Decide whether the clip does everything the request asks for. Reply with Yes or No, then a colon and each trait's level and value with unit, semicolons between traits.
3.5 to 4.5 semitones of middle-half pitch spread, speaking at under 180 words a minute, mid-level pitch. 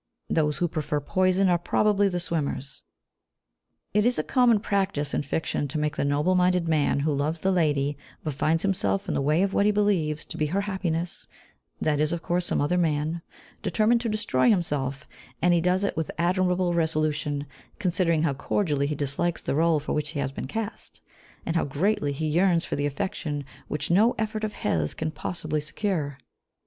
No: average, 4.2 semitones; average, 195 wpm; medium, 165 Hz